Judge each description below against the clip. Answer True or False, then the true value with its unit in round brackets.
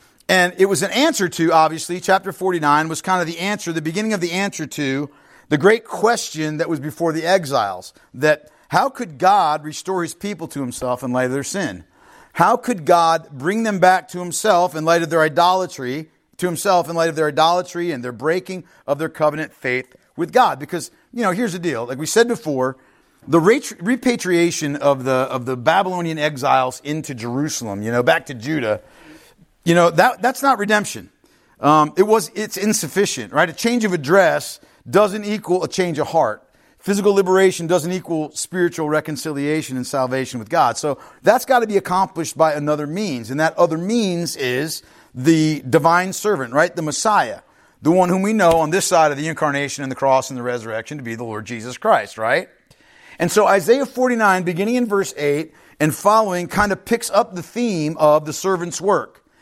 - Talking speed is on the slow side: False (195 wpm)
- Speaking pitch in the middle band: True (170 Hz)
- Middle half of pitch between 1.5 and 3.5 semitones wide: False (4.6 semitones)